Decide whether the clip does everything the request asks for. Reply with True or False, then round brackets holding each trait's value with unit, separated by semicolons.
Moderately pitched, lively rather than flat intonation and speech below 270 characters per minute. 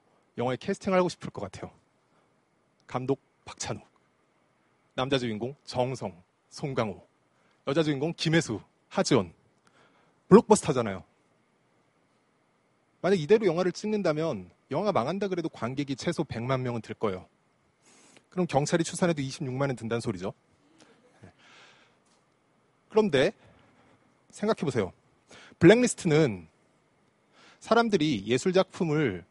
True (150 Hz; 7.0 semitones; 250 characters per minute)